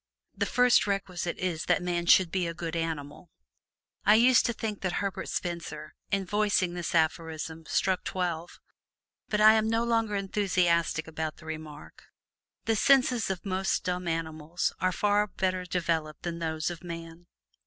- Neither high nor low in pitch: Yes, medium, 175 Hz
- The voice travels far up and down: No, average, 3.6 semitones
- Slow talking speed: No, average, 160 wpm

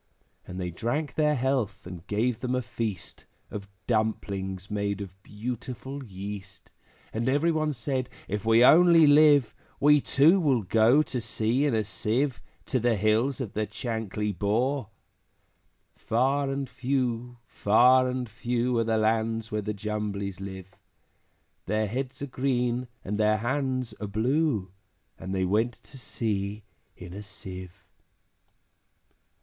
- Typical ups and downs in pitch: Yes, average, 4.0 semitones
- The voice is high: No, low, 115 Hz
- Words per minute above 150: No, average, 145 wpm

